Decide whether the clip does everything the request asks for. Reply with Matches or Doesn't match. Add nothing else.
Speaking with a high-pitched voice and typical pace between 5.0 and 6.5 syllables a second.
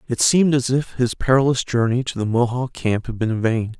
Doesn't match